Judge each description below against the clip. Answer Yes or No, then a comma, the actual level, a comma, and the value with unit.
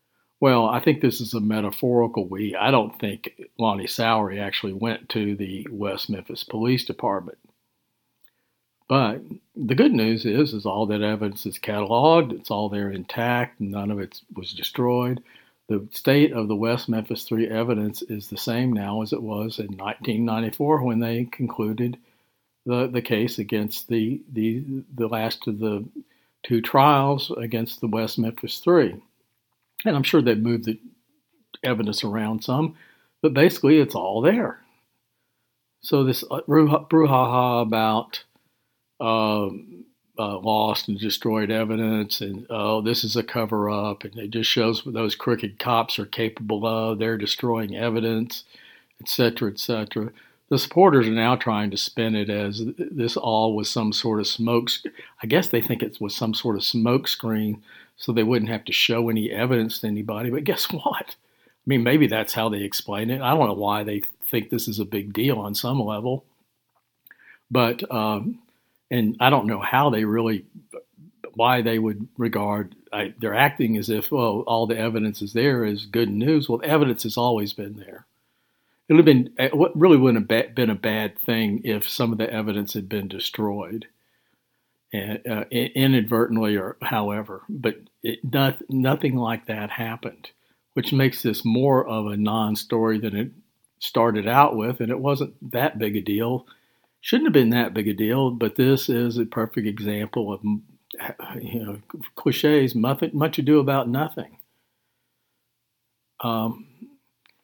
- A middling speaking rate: Yes, average, 165 wpm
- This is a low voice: Yes, low, 115 Hz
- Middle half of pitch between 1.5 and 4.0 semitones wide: Yes, narrow, 2.5 semitones